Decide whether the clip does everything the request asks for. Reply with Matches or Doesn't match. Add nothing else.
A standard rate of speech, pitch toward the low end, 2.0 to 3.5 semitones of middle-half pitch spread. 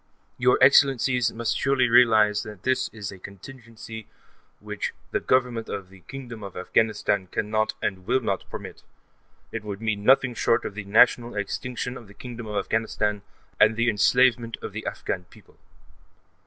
Matches